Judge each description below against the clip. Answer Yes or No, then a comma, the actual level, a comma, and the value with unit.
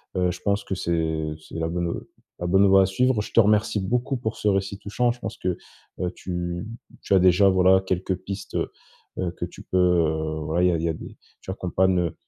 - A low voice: Yes, very low, 95 Hz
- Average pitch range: No, narrow, 2.3 semitones